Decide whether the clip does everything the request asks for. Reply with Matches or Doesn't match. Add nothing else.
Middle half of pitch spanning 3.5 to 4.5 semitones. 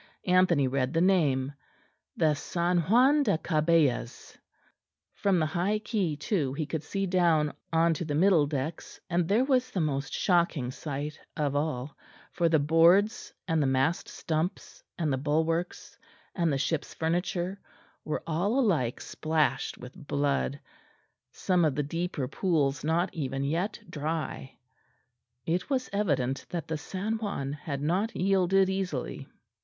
Matches